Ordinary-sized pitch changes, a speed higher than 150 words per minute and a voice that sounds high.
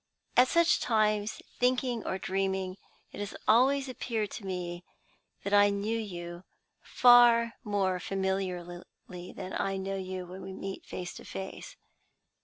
No: average, 3.5 semitones; average, 140 wpm; high, 195 Hz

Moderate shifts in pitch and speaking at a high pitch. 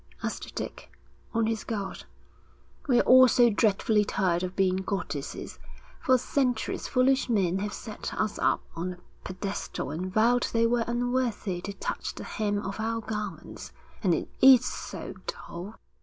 Yes: average, 4.0 semitones; high, 215 Hz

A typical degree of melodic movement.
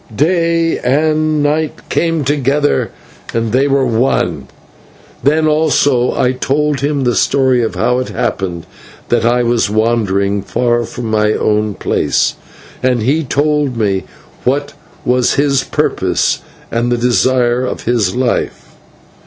Yes: average, 3.8 semitones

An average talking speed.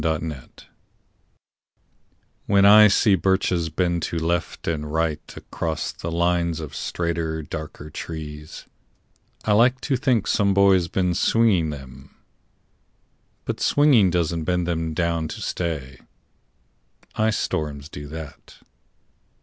No: slow, 115 wpm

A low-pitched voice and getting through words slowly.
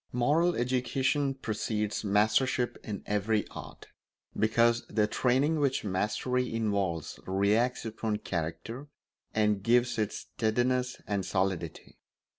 Yes: low, 110 Hz; slow, 105 wpm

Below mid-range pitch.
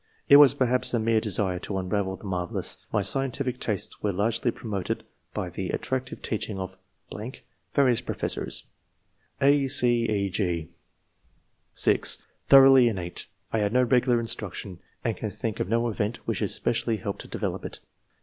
Yes: low, 115 Hz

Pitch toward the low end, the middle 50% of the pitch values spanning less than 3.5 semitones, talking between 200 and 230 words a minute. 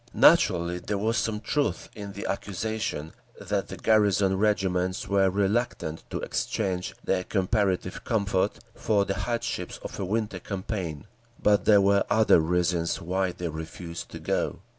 No: very low, 95 Hz; average, 2.7 semitones; average, 145 wpm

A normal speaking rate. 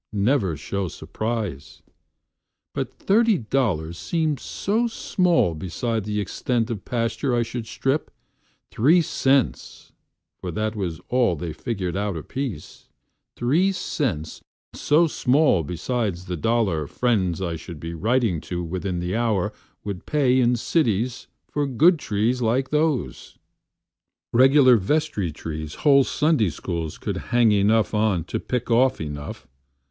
No: slow, 115 wpm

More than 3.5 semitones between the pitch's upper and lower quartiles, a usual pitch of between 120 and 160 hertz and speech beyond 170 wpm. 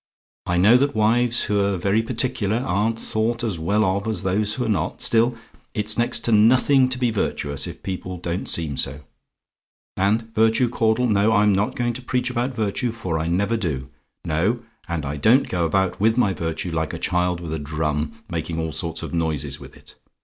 No: average, 5.3 semitones; low, 105 Hz; average, 195 wpm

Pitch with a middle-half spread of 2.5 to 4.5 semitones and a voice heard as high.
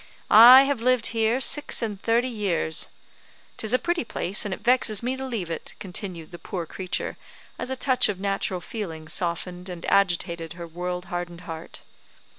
No: average, 5.2 semitones; high, 195 Hz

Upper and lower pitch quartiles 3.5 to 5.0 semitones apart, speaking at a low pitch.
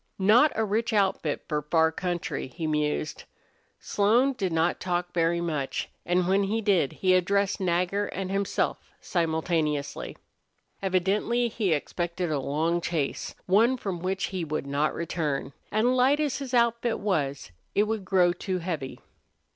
No: average, 4.2 semitones; medium, 180 Hz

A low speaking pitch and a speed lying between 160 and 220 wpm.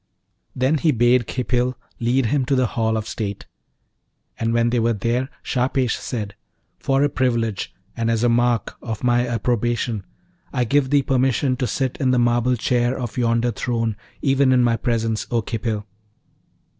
Yes: low, 120 Hz; average, 170 wpm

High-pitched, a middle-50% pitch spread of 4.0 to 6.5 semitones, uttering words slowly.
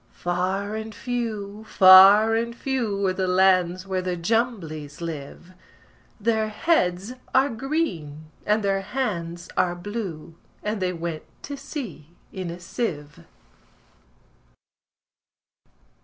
Yes: high, 195 Hz; average, 4.3 semitones; slow, 110 wpm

